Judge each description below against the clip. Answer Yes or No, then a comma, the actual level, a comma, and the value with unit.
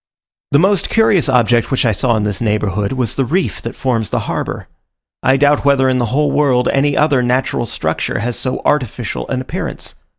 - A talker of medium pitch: No, low, 130 Hz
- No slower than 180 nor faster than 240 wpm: Yes, average, 195 wpm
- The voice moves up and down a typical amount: Yes, average, 3.3 semitones